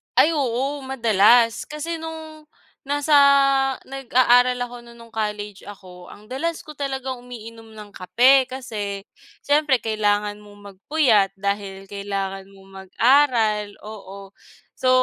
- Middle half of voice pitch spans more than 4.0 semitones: Yes, average, 4.6 semitones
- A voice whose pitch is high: Yes, high, 230 Hz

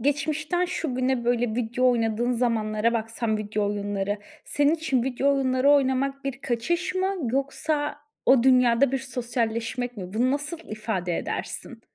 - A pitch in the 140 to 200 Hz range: No, very high, 250 Hz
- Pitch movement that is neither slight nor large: Yes, average, 3.6 semitones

